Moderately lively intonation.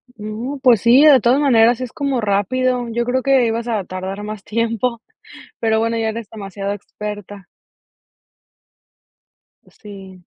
Yes: average, 3.1 semitones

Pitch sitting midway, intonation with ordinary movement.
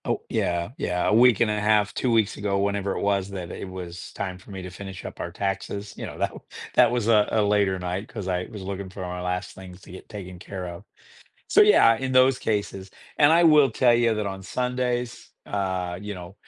No: low, 100 Hz; average, 3.2 semitones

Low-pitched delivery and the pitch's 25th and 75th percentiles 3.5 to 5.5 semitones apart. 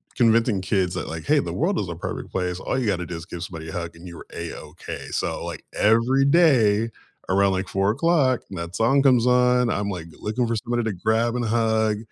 Yes: low, 110 Hz; average, 4.8 semitones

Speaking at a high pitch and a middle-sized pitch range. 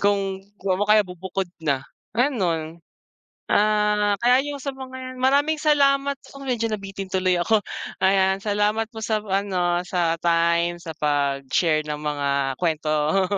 Yes: high, 195 Hz; average, 4.6 semitones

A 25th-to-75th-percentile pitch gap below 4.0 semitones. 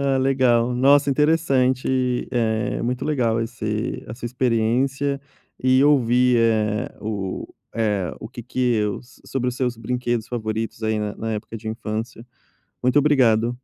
Yes: average, 2.8 semitones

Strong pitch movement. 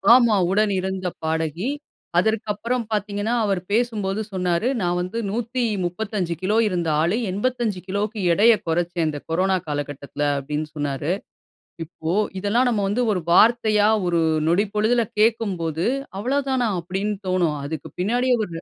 No: average, 4.2 semitones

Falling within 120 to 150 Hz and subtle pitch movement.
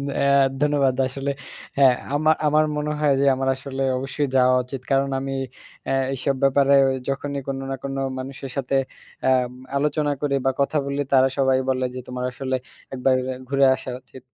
Yes: low, 135 Hz; narrow, 1.2 semitones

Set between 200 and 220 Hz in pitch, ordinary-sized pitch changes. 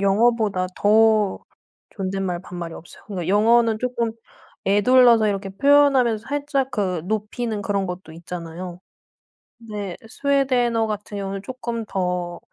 Yes: high, 210 Hz; average, 3.9 semitones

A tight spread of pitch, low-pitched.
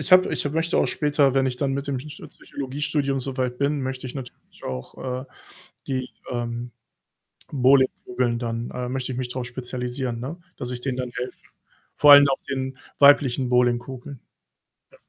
Yes: narrow, 2.0 semitones; low, 130 Hz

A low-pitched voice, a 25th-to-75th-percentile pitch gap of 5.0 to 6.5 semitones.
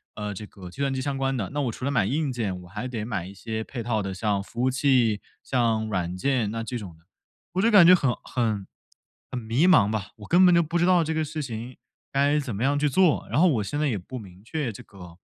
Yes: low, 120 Hz; wide, 5.5 semitones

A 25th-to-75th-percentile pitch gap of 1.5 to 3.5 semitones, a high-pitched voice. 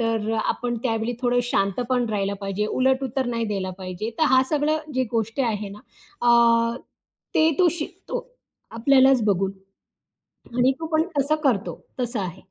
No: average, 4.2 semitones; high, 240 Hz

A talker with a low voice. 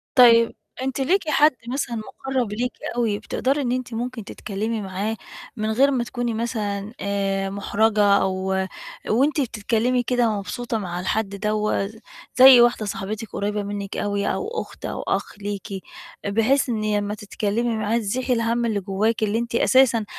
No: high, 225 Hz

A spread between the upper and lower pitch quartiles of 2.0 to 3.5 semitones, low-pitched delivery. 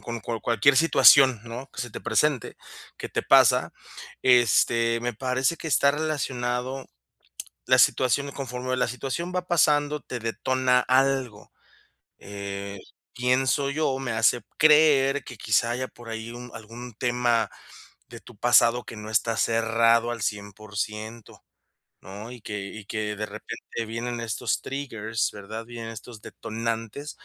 Yes: average, 2.8 semitones; low, 120 Hz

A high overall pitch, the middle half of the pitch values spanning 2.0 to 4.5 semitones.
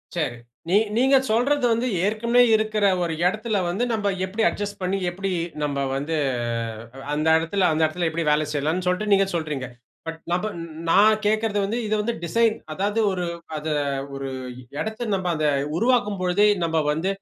No: high, 195 Hz; average, 5.0 semitones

